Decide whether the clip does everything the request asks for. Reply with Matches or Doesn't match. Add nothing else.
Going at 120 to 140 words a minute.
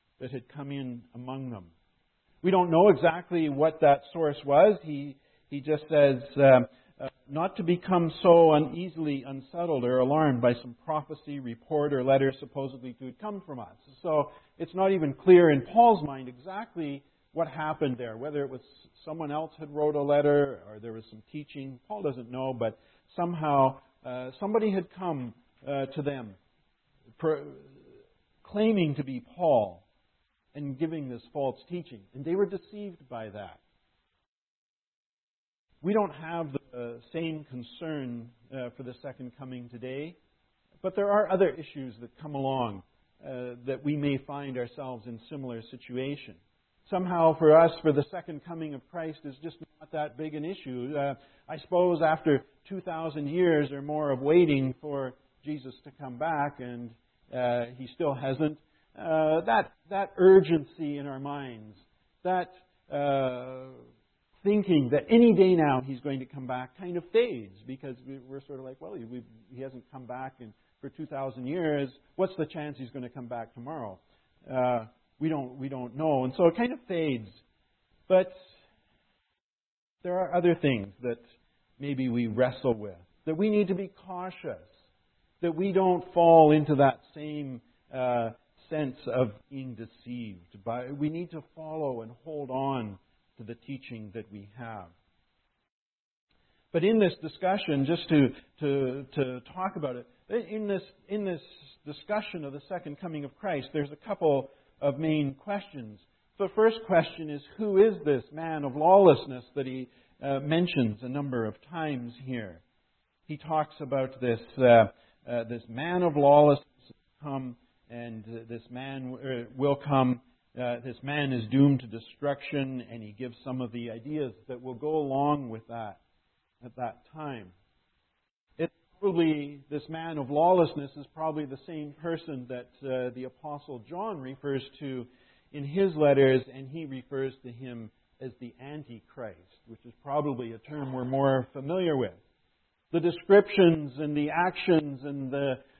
Doesn't match